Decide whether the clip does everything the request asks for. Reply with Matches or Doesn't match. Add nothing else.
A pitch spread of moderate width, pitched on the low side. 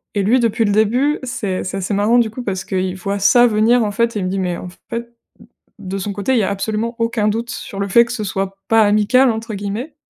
Doesn't match